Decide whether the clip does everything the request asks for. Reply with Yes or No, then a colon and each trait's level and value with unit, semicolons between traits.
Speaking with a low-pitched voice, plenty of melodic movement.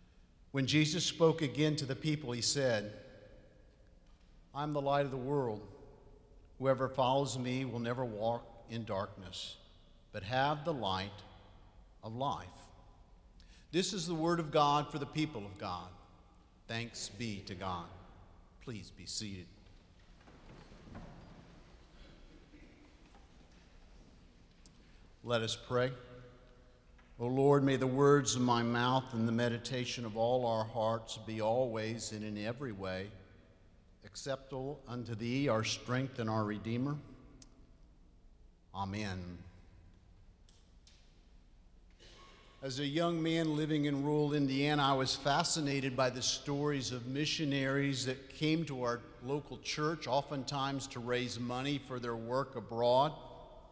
Yes: low, 120 Hz; wide, 6.3 semitones